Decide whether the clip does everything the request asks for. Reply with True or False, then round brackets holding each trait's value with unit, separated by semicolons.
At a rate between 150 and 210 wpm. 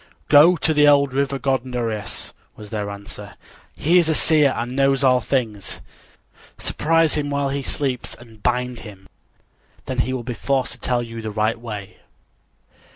True (170 wpm)